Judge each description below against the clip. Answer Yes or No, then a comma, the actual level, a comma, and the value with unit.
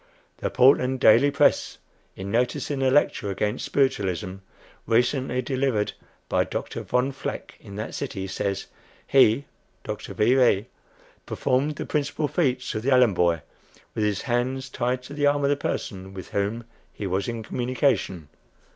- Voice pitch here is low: Yes, low, 125 Hz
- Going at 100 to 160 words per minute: Yes, average, 155 wpm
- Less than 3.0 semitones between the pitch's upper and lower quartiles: No, average, 4.7 semitones